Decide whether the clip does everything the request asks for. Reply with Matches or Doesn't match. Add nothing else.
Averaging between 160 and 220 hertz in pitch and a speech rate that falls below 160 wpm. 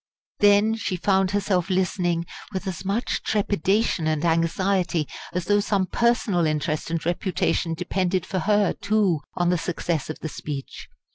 Matches